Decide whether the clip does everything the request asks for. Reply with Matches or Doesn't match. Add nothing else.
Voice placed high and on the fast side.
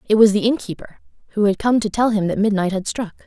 Matches